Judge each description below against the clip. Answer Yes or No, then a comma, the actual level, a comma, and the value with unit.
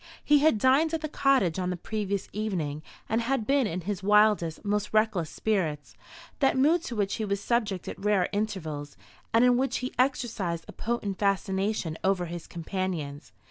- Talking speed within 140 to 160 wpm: No, average, 180 wpm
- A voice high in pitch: Yes, high, 205 Hz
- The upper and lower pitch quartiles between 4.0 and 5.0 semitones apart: Yes, average, 4.7 semitones